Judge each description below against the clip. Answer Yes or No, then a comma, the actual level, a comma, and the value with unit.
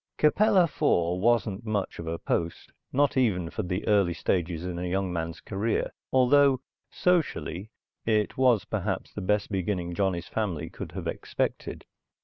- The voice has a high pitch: No, low, 100 Hz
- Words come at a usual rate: Yes, average, 150 wpm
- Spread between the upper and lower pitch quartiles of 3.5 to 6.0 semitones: Yes, wide, 5.4 semitones